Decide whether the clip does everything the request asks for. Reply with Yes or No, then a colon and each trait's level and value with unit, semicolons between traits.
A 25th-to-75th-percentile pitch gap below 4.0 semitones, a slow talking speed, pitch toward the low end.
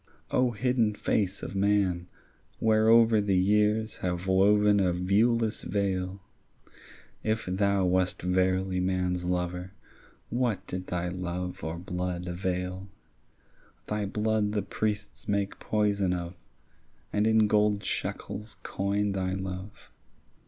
Yes: narrow, 2.5 semitones; slow, 115 wpm; very low, 95 Hz